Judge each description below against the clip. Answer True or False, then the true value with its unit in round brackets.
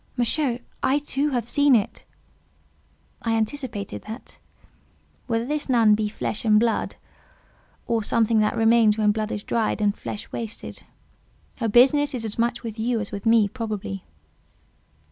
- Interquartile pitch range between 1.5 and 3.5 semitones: True (2.4 semitones)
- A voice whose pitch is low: False (225 Hz)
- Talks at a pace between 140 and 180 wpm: True (155 wpm)